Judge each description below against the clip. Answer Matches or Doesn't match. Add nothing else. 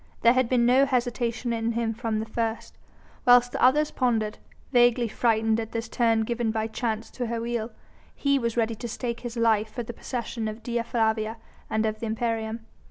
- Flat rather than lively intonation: Matches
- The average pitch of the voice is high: Matches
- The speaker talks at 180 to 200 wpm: Matches